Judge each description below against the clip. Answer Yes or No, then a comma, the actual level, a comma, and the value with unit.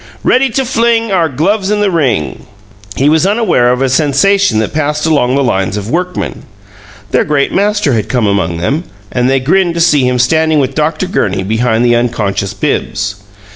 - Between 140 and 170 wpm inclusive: No, average, 185 wpm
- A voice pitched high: No, medium, 140 Hz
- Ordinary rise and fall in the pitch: No, wide, 7.2 semitones